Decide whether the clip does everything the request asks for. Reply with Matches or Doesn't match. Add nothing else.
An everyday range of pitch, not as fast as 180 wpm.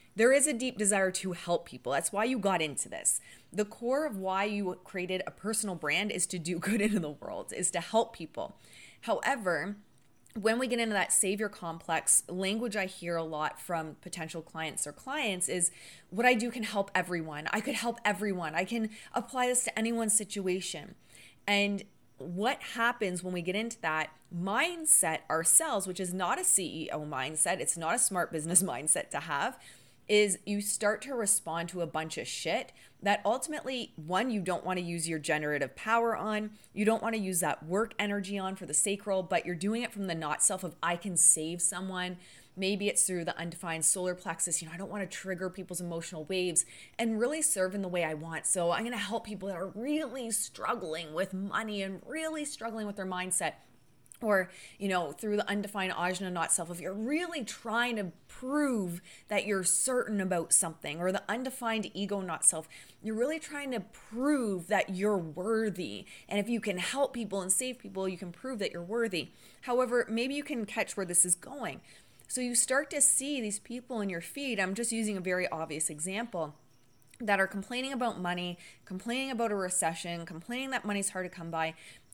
Doesn't match